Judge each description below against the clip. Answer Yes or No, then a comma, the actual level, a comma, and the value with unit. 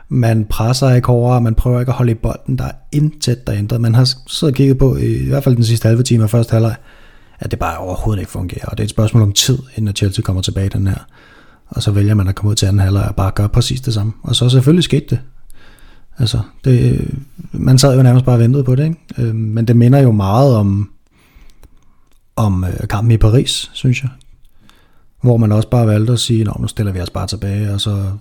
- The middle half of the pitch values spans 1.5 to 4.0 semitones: Yes, average, 3.5 semitones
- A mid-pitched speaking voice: No, low, 115 Hz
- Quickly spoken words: Yes, fast, 240 wpm